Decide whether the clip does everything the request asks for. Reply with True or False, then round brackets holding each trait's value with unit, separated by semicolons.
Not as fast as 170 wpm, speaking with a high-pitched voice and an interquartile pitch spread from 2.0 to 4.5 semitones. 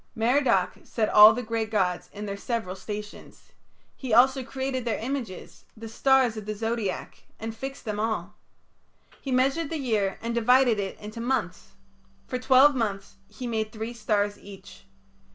True (160 wpm; 225 Hz; 3.4 semitones)